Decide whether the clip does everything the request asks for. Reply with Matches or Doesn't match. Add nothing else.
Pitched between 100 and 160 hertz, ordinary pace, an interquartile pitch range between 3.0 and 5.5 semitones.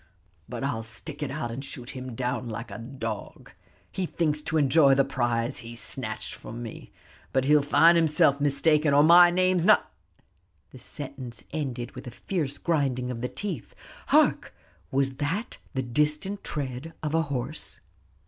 Matches